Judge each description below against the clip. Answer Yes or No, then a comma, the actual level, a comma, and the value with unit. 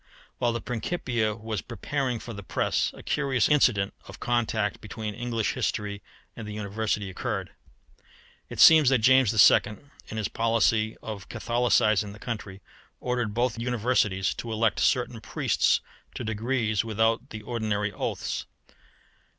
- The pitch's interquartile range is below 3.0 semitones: Yes, narrow, 2.4 semitones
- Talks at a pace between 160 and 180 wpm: No, average, 140 wpm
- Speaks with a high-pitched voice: No, low, 110 Hz